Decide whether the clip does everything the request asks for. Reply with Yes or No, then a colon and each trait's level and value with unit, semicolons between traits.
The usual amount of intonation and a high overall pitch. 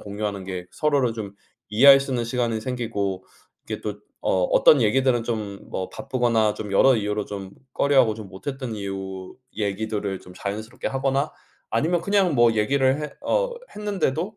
No: average, 4.9 semitones; low, 115 Hz